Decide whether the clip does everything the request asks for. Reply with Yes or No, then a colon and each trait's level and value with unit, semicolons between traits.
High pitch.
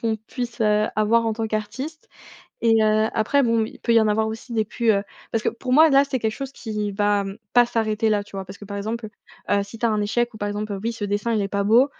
Yes: high, 220 Hz